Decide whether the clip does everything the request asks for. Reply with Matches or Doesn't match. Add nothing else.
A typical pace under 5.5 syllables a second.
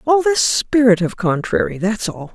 Matches